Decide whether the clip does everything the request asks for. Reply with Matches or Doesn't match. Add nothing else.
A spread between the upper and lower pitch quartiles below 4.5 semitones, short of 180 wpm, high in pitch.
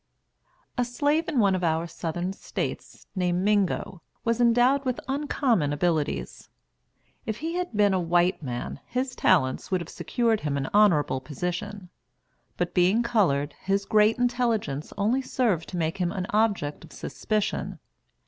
Doesn't match